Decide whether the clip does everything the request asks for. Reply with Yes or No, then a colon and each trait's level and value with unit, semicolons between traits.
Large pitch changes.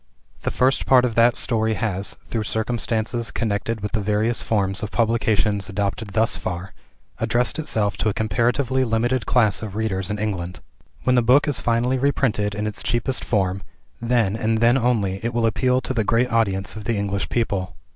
No: average, 2.7 semitones